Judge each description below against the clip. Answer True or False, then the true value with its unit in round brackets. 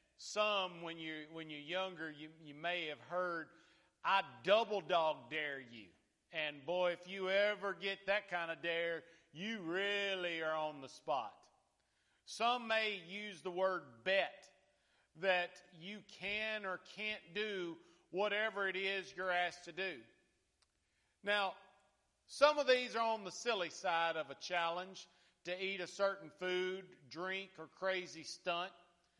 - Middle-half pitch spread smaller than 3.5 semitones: True (2.9 semitones)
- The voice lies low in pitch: False (180 Hz)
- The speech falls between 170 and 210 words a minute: False (150 wpm)